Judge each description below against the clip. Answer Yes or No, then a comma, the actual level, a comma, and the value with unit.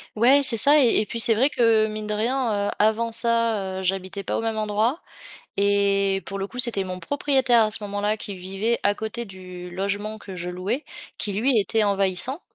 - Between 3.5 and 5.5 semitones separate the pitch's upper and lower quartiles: No, average, 2.9 semitones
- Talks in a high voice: Yes, high, 215 Hz